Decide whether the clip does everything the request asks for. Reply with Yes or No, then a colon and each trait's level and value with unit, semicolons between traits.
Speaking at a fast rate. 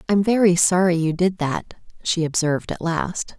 No: average, 175 wpm